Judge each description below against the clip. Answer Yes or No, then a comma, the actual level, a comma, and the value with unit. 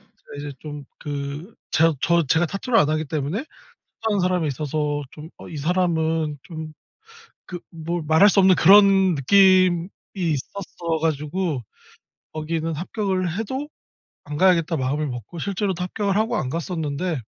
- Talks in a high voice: No, medium, 165 Hz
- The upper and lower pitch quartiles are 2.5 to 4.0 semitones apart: Yes, average, 3.7 semitones